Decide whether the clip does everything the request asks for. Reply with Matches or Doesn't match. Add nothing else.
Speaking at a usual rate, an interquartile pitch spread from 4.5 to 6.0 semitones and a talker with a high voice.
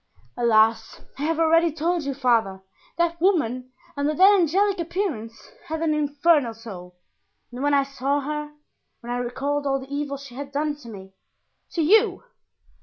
Matches